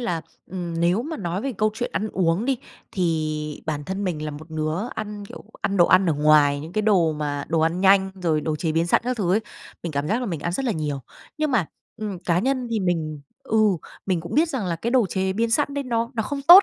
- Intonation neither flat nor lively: No, wide, 5.7 semitones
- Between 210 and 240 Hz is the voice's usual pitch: No, medium, 185 Hz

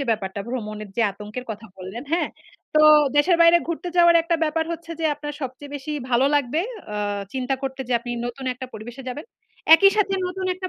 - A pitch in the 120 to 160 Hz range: No, very high, 270 Hz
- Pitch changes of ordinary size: No, wide, 5.7 semitones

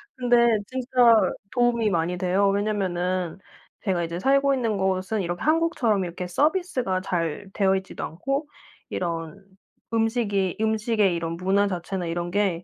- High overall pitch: Yes, high, 195 Hz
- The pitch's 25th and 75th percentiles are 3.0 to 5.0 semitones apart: Yes, average, 4.7 semitones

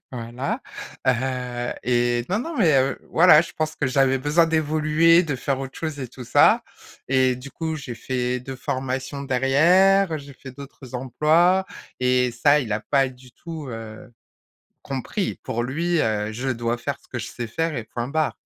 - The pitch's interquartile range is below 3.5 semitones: No, average, 4.0 semitones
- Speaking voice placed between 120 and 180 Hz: Yes, low, 135 Hz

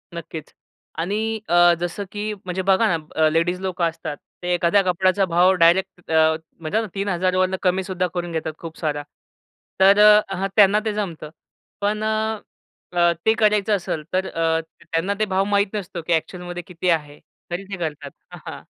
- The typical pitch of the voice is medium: Yes, medium, 180 Hz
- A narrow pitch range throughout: No, average, 3.2 semitones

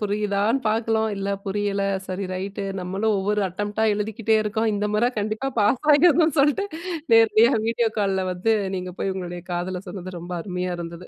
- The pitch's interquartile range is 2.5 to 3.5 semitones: Yes, average, 3.0 semitones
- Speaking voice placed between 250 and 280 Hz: No, high, 205 Hz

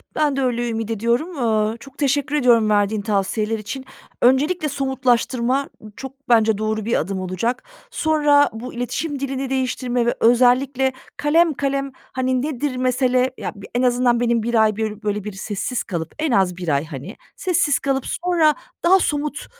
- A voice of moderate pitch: No, very high, 250 Hz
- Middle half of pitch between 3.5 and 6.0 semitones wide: Yes, average, 4.0 semitones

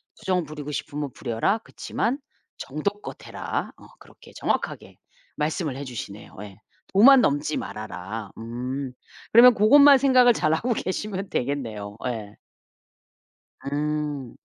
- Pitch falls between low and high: Yes, medium, 150 Hz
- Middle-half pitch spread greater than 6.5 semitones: Yes, wide, 9.0 semitones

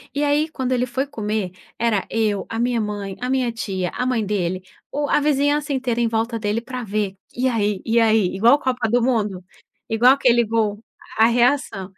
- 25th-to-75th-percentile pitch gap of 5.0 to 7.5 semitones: No, average, 3.4 semitones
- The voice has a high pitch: Yes, high, 230 Hz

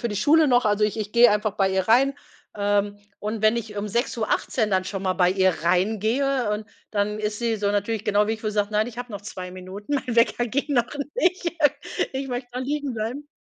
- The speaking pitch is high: Yes, high, 215 Hz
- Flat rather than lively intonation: No, average, 3.1 semitones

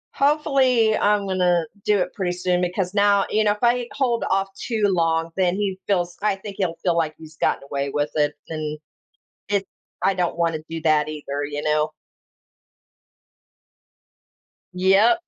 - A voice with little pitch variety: No, average, 4.1 semitones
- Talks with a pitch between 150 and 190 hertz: Yes, medium, 185 Hz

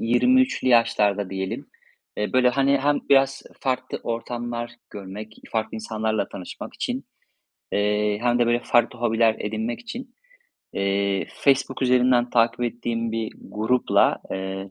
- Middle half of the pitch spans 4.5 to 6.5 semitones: No, average, 3.0 semitones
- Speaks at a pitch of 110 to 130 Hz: Yes, low, 115 Hz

